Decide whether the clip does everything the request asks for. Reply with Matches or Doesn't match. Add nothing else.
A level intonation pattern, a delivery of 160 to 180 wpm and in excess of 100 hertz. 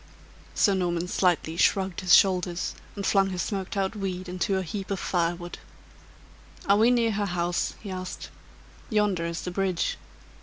Matches